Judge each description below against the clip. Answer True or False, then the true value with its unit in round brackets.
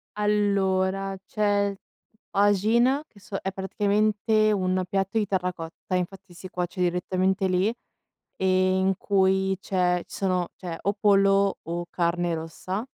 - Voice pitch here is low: False (190 Hz)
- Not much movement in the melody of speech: True (1.8 semitones)